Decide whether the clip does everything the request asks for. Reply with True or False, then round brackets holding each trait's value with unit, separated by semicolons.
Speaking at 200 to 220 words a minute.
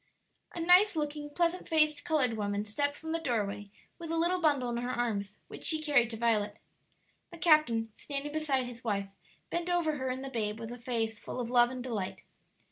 True (205 wpm)